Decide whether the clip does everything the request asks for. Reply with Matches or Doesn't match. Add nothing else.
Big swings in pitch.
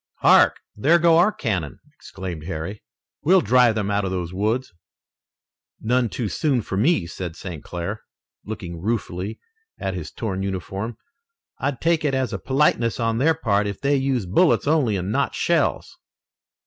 Matches